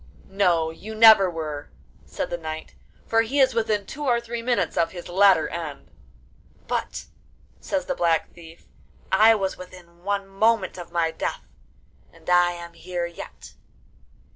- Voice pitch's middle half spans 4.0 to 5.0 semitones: Yes, average, 4.5 semitones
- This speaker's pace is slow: No, average, 155 wpm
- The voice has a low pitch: No, medium, 185 Hz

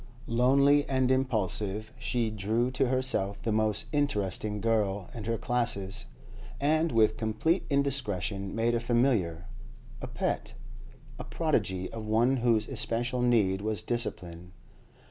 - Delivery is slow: Yes, slow, 125 wpm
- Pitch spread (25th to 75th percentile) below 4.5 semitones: Yes, average, 3.6 semitones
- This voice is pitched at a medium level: No, low, 115 Hz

